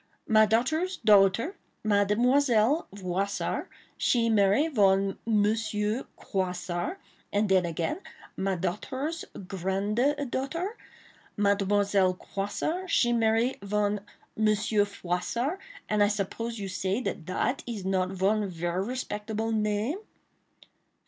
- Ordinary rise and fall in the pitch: Yes, average, 3.3 semitones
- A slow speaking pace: Yes, slow, 105 wpm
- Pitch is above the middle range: Yes, high, 210 Hz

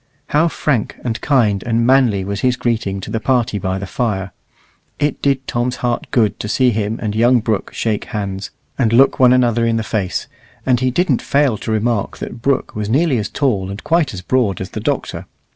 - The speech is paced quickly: Yes, fast, 210 wpm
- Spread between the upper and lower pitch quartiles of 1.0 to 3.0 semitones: No, average, 3.8 semitones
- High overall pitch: No, low, 115 Hz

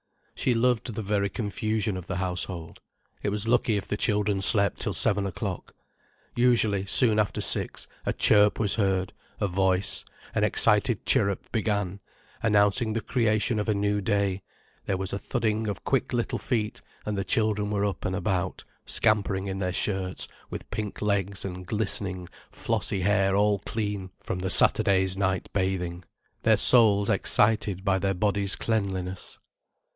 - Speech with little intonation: Yes, narrow, 2.1 semitones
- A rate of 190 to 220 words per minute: No, average, 160 wpm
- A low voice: Yes, low, 100 Hz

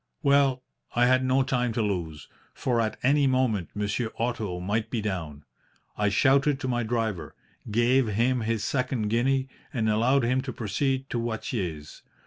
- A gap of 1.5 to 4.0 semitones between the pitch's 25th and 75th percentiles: Yes, average, 3.7 semitones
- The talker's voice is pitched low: Yes, low, 120 Hz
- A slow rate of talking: No, average, 160 wpm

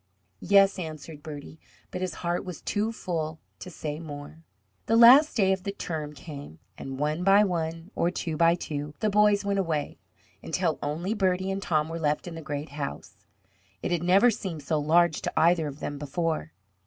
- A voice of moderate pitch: Yes, medium, 165 Hz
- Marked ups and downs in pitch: No, average, 4.1 semitones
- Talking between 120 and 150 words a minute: No, average, 190 wpm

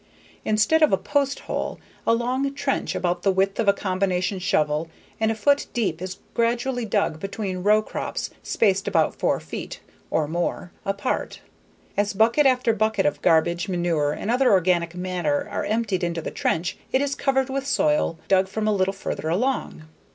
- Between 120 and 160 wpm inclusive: No, average, 175 wpm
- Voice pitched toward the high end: Yes, high, 200 Hz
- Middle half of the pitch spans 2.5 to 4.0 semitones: No, average, 4.7 semitones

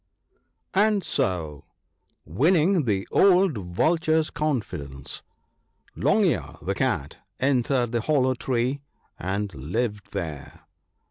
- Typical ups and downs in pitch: No, wide, 9.0 semitones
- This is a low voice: Yes, low, 120 Hz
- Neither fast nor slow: No, slow, 110 wpm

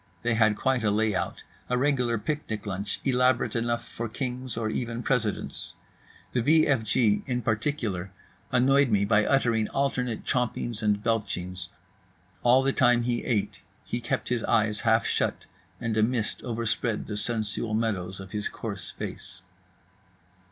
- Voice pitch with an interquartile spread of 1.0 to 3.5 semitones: Yes, average, 2.7 semitones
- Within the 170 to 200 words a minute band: No, average, 150 wpm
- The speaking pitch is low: Yes, low, 115 Hz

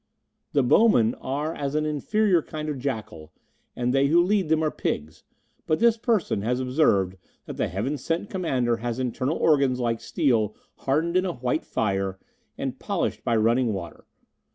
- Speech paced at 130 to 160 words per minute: No, average, 170 wpm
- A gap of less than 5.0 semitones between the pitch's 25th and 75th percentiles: No, wide, 5.6 semitones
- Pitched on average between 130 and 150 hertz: Yes, low, 135 Hz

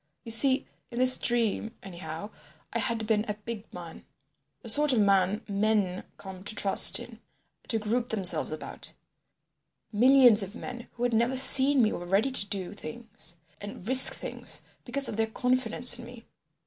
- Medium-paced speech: Yes, average, 160 wpm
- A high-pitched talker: Yes, high, 220 Hz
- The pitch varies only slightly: No, average, 3.5 semitones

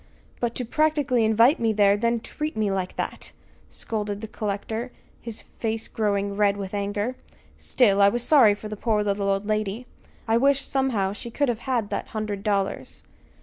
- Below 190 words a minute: Yes, average, 180 wpm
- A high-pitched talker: Yes, high, 215 Hz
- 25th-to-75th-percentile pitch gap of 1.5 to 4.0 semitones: Yes, average, 2.9 semitones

